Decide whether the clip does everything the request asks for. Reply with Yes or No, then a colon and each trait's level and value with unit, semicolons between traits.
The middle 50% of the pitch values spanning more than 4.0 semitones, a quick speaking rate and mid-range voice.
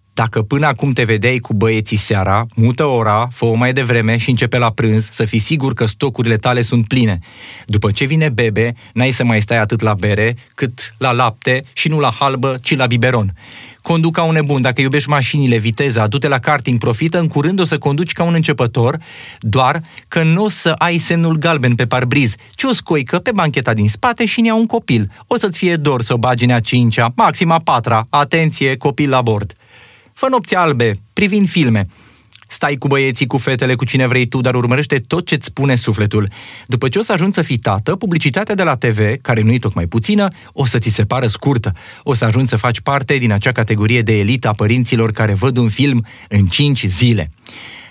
No: average, 4.6 semitones; fast, 210 wpm; low, 125 Hz